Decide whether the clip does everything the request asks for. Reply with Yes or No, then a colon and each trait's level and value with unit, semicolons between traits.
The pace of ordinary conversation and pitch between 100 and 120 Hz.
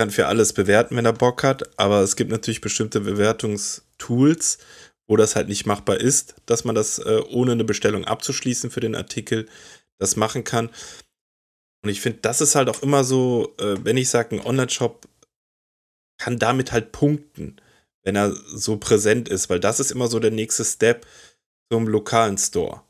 Yes: average, 175 wpm; low, 115 Hz